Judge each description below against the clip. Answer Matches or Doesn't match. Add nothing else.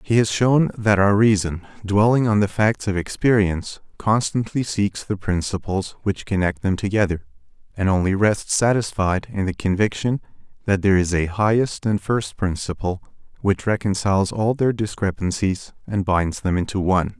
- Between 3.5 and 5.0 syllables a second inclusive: Matches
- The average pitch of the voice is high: Doesn't match